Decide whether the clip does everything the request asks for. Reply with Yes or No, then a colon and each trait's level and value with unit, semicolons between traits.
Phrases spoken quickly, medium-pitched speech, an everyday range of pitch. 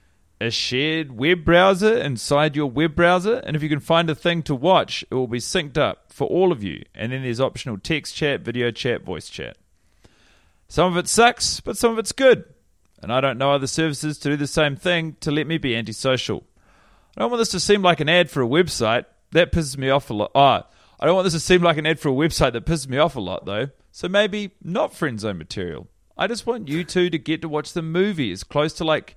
Yes: fast, 245 wpm; medium, 155 Hz; average, 5.0 semitones